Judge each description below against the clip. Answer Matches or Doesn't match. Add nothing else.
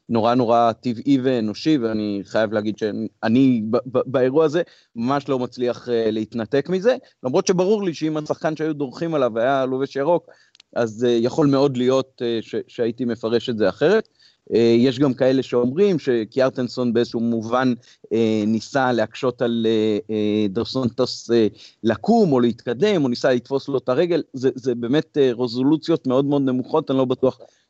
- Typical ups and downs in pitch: Matches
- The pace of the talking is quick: Matches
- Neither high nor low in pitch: Doesn't match